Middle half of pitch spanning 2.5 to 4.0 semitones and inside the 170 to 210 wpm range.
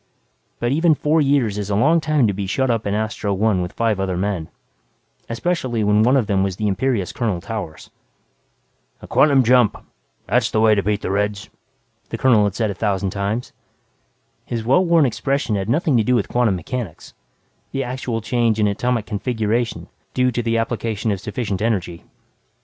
Yes: average, 3.7 semitones; average, 185 wpm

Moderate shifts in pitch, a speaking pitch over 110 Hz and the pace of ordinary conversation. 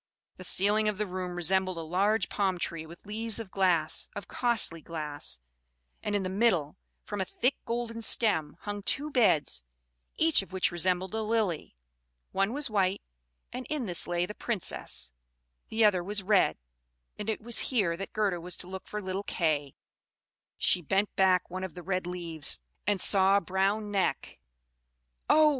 Yes: average, 3.3 semitones; high, 190 Hz; average, 175 wpm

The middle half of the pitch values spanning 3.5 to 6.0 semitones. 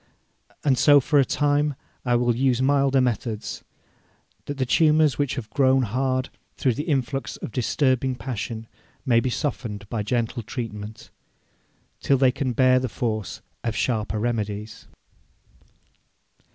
No: average, 3.0 semitones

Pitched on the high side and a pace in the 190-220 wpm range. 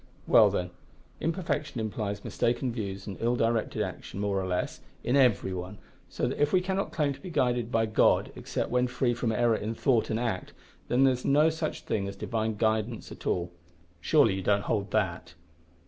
No: low, 115 Hz; average, 195 wpm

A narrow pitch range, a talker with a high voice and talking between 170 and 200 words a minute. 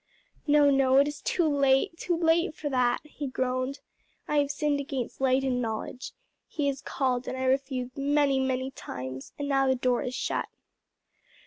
Yes: narrow, 2.1 semitones; very high, 270 Hz; average, 180 wpm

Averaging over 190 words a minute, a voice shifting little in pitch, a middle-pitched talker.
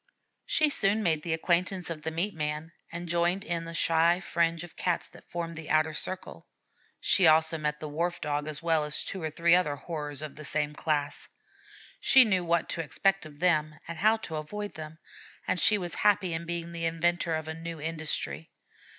Yes: average, 200 wpm; narrow, 2.1 semitones; medium, 165 Hz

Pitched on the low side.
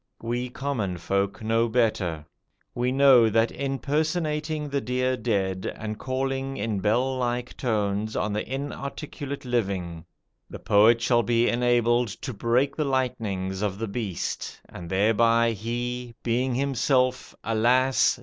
Yes: low, 120 Hz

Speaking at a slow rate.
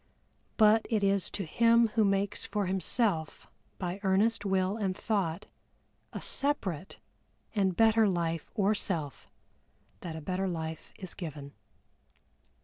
Yes: slow, 130 wpm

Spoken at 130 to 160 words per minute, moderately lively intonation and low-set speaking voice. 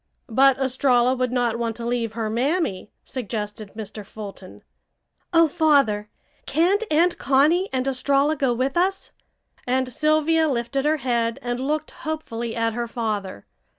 No: average, 145 wpm; average, 4.7 semitones; very high, 255 Hz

